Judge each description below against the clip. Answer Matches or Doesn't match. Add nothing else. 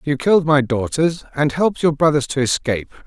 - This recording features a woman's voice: Doesn't match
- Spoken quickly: Doesn't match